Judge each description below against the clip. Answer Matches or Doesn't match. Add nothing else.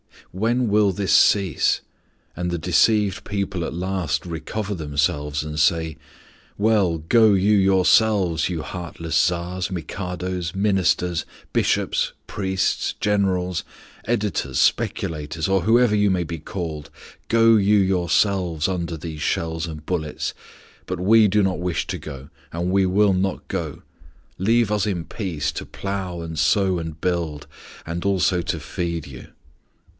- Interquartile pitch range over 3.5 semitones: Doesn't match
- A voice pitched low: Matches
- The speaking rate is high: Doesn't match